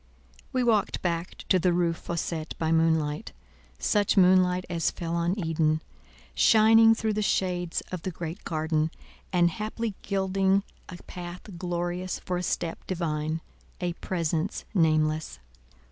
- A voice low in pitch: No, medium, 175 Hz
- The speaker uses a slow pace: Yes, slow, 125 wpm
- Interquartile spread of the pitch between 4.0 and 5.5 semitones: No, average, 2.8 semitones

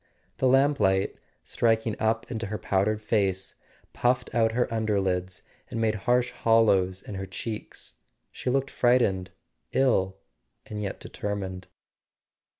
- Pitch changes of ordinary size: Yes, average, 3.4 semitones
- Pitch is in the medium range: No, low, 110 Hz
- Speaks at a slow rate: Yes, slow, 125 wpm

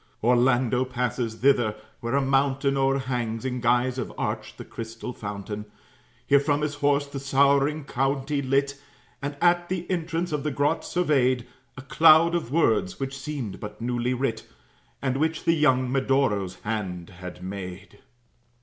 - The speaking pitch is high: No, low, 135 Hz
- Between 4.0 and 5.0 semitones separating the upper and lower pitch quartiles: No, average, 3.3 semitones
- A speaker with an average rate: Yes, average, 150 wpm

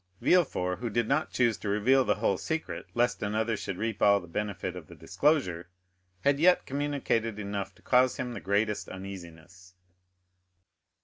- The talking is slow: No, average, 165 wpm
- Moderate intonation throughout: Yes, average, 4.8 semitones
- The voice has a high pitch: No, low, 105 Hz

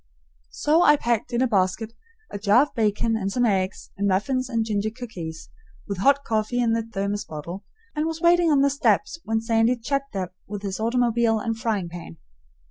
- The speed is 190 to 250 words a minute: Yes, average, 195 wpm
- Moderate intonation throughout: Yes, average, 3.8 semitones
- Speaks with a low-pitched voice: No, high, 225 Hz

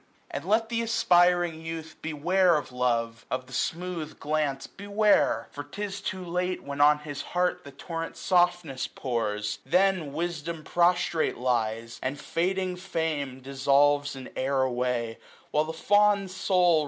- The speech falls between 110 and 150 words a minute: Yes, average, 145 wpm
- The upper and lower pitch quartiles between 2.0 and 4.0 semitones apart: No, average, 5.1 semitones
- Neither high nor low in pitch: Yes, medium, 160 Hz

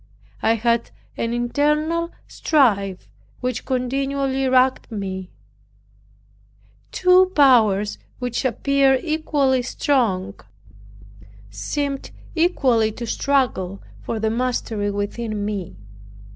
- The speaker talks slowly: Yes, slow, 90 wpm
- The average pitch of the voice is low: No, very high, 250 Hz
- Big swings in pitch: No, average, 4.6 semitones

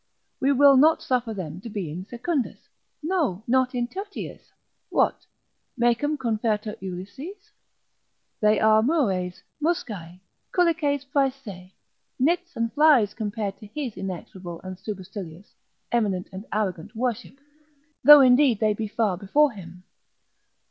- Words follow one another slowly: Yes, slow, 130 wpm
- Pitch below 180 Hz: No, high, 225 Hz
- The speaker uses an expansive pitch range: Yes, wide, 6.3 semitones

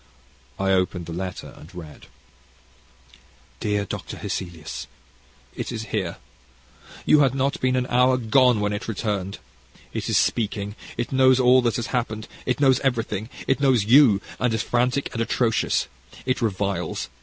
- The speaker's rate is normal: Yes, average, 155 wpm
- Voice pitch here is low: Yes, low, 115 Hz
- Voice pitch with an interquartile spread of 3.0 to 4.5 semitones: Yes, average, 4.2 semitones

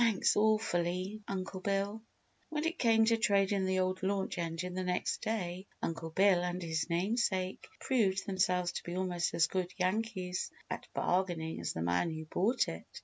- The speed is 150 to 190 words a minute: Yes, average, 170 wpm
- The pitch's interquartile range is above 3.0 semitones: No, narrow, 2.5 semitones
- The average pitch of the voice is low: No, medium, 185 Hz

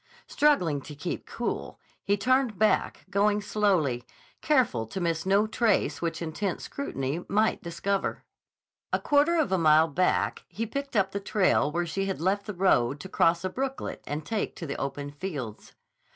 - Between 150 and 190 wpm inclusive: Yes, average, 170 wpm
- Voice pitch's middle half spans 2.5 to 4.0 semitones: No, average, 5.2 semitones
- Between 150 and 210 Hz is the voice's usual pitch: Yes, high, 190 Hz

